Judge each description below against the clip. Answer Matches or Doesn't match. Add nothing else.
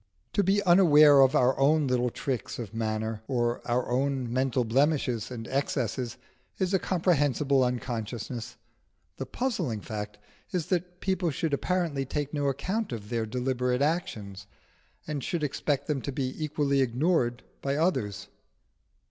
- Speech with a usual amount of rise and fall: Matches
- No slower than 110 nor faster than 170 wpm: Matches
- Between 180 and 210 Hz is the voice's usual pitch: Doesn't match